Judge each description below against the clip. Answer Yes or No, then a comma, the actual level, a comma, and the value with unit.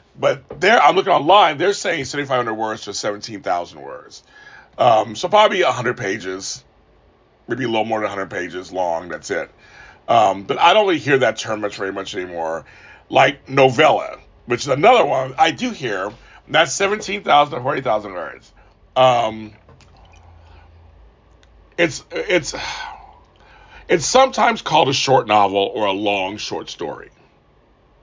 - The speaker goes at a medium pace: Yes, average, 145 wpm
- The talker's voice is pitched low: Yes, low, 110 Hz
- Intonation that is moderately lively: No, wide, 6.4 semitones